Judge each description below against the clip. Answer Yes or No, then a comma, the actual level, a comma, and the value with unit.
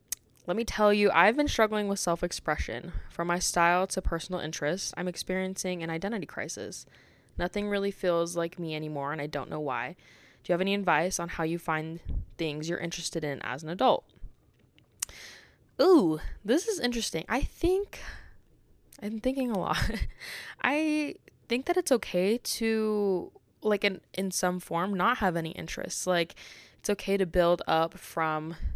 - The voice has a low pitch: No, medium, 185 Hz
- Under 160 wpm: No, average, 165 wpm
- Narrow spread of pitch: No, average, 3.8 semitones